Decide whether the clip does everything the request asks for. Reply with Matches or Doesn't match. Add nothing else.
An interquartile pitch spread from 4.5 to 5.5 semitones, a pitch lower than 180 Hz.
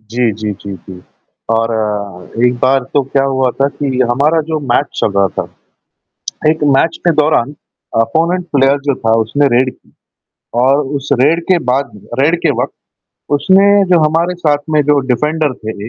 Matches